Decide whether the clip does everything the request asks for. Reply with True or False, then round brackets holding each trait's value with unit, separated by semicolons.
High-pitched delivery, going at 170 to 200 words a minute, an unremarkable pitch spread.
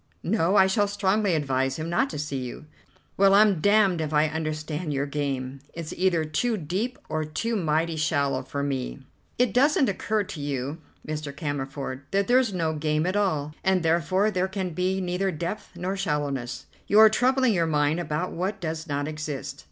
False (165 Hz; 185 wpm; 4.7 semitones)